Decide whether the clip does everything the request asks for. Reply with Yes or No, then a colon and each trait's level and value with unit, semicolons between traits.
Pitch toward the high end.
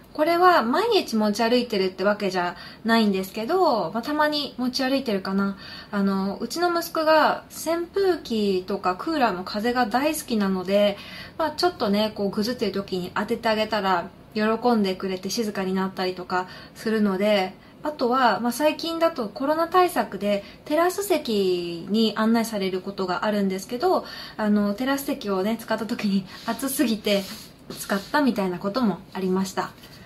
Yes: high, 220 Hz